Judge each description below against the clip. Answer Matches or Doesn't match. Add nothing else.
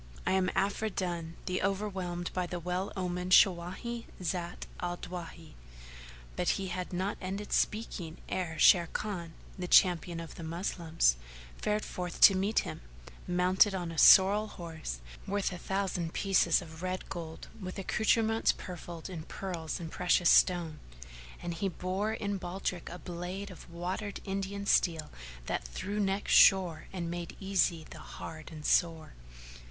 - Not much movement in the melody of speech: Matches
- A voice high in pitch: Doesn't match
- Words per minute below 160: Matches